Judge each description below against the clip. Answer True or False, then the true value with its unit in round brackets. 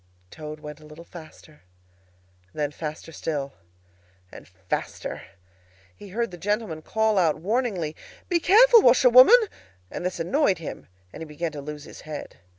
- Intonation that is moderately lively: False (6.4 semitones)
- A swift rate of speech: False (150 wpm)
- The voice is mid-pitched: True (165 Hz)